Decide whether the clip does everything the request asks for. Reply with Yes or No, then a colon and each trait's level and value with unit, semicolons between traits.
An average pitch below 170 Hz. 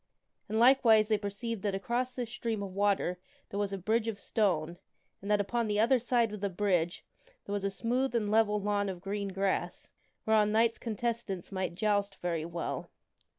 No: high, 205 Hz